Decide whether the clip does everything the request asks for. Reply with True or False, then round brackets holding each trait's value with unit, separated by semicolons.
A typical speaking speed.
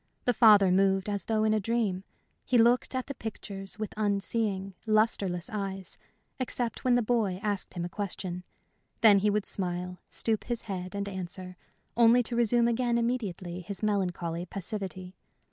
True (160 wpm)